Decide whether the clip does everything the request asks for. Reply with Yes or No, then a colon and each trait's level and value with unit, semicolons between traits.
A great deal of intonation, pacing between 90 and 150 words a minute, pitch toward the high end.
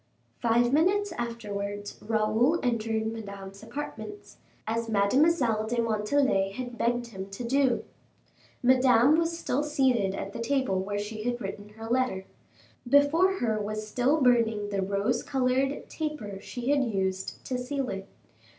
No: average, 4.3 semitones; average, 140 wpm; high, 235 Hz